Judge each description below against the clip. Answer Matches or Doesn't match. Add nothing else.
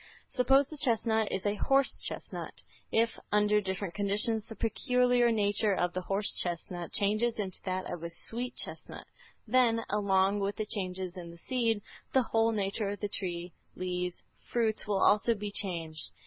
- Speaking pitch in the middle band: Doesn't match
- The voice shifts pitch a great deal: Doesn't match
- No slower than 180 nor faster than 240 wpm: Doesn't match